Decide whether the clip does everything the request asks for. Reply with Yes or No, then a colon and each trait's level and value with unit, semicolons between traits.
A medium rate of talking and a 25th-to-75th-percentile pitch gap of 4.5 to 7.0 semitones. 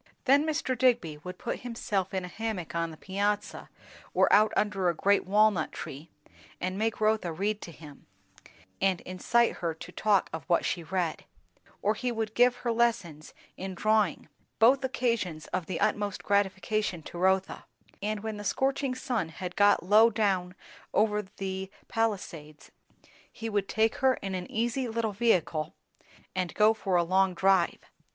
No: average, 165 wpm; average, 3.6 semitones